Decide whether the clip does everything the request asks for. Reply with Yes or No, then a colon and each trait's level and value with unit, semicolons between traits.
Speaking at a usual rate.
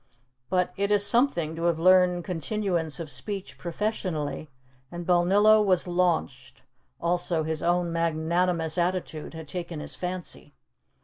No: slow, 130 wpm